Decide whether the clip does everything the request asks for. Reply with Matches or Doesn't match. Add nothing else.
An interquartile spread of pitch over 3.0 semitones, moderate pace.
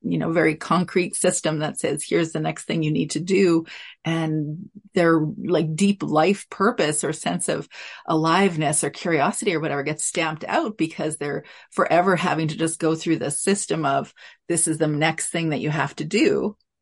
Doesn't match